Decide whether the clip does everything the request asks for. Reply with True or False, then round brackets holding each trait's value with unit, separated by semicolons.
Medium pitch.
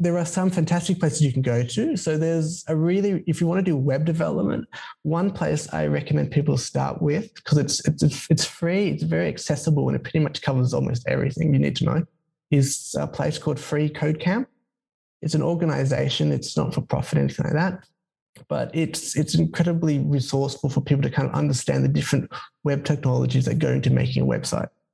True (150 Hz)